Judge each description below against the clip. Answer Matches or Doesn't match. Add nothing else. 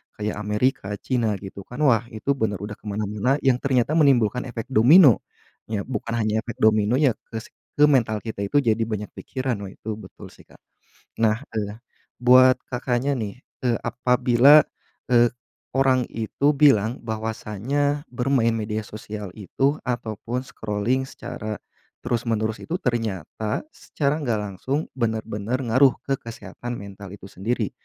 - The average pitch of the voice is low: Matches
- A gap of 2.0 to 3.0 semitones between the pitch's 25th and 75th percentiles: Doesn't match